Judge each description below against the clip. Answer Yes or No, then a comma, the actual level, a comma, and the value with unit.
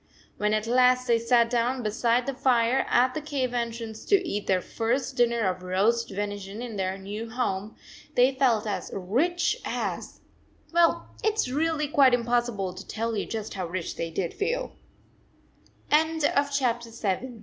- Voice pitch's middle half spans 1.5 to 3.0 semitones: No, average, 4.1 semitones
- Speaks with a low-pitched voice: No, high, 235 Hz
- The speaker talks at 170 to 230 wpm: No, average, 155 wpm